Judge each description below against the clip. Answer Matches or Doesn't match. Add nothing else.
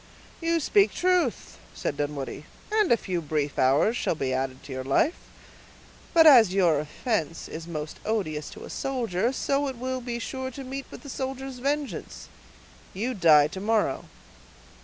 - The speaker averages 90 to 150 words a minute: Doesn't match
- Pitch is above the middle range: Matches